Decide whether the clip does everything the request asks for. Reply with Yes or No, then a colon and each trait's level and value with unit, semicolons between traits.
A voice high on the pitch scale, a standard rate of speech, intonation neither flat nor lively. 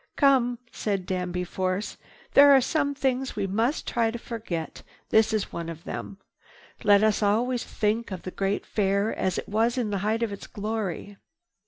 Yes: high, 210 Hz; average, 180 wpm; average, 3.4 semitones